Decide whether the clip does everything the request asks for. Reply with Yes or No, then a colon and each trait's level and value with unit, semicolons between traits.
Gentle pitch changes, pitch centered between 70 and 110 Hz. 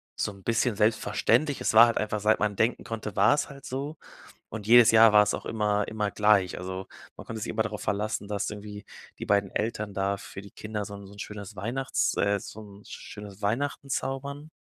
Yes: narrow, 2.1 semitones; low, 105 Hz